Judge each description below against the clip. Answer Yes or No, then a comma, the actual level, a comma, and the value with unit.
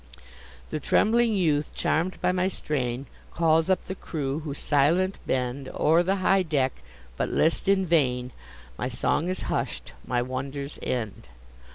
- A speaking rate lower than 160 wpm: Yes, average, 150 wpm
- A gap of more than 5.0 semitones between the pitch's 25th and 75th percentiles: Yes, wide, 5.5 semitones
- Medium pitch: Yes, medium, 155 Hz